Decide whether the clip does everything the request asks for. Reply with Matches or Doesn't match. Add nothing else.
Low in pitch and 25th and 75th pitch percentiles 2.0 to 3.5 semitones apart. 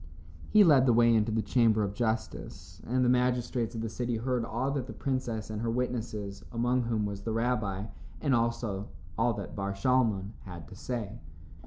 Matches